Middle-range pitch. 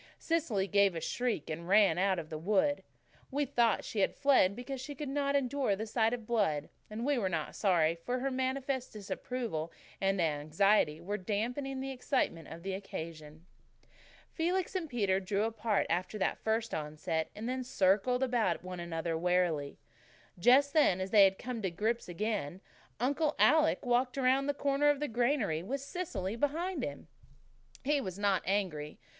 No: high, 215 Hz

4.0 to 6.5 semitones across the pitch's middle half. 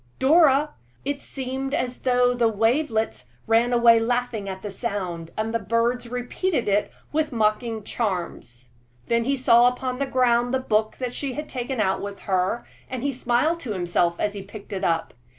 No: average, 3.6 semitones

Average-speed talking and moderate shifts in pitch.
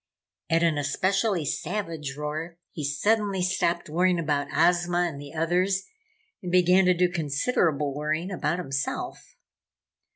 No: slow, 130 wpm; average, 3.4 semitones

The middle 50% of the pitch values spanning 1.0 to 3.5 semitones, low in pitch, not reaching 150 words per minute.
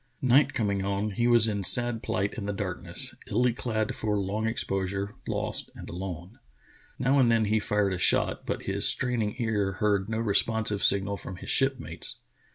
No: average, 2.8 semitones; low, 105 Hz; average, 180 wpm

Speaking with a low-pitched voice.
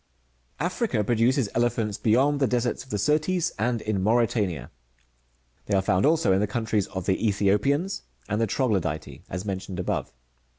Yes: low, 110 Hz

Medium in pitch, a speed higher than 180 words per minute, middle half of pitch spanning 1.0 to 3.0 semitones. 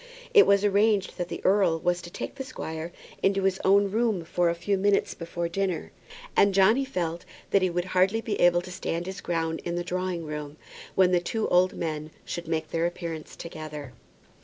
Yes: medium, 180 Hz; average, 200 wpm; average, 2.7 semitones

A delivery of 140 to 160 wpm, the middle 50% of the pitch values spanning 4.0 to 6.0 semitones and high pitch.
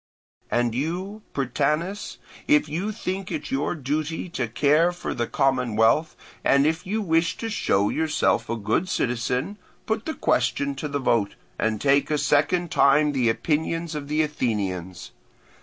No: average, 155 wpm; average, 5.3 semitones; medium, 150 Hz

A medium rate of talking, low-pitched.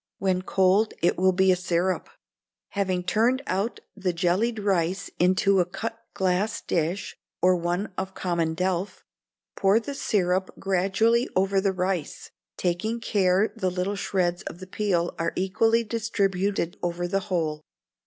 No: average, 145 wpm; high, 190 Hz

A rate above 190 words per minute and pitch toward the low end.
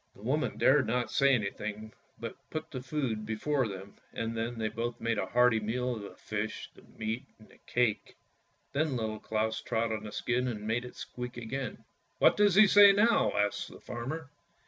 Yes: fast, 205 wpm; low, 120 Hz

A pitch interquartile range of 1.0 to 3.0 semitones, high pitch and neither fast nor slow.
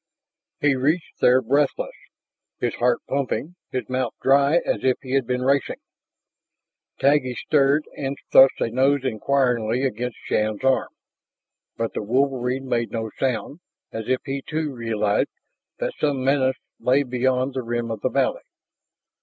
No: narrow, 2.4 semitones; low, 130 Hz; average, 145 wpm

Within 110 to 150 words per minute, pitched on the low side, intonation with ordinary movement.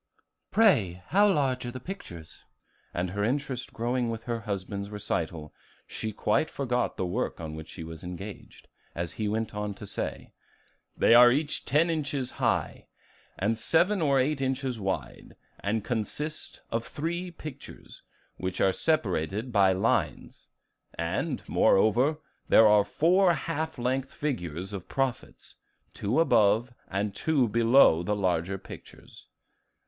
No: average, 140 wpm; low, 115 Hz; wide, 6.1 semitones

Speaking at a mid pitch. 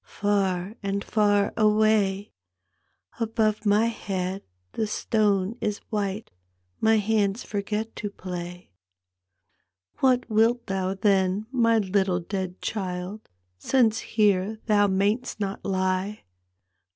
No: high, 205 Hz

